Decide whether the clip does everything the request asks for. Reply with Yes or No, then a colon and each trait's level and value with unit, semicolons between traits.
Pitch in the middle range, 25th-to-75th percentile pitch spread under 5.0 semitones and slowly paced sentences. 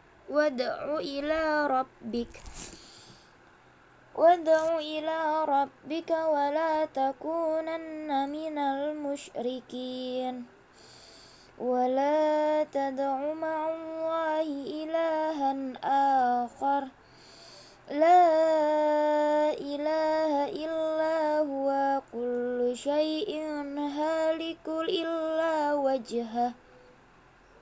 No: very high, 300 Hz; narrow, 2.6 semitones; slow, 55 wpm